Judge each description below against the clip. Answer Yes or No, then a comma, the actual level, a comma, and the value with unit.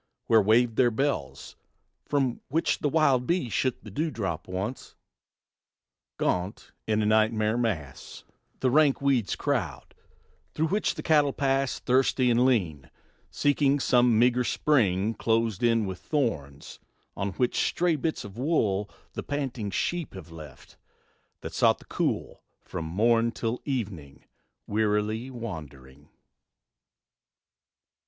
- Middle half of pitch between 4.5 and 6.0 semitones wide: Yes, average, 5.2 semitones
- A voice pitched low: Yes, low, 115 Hz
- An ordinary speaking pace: No, slow, 130 wpm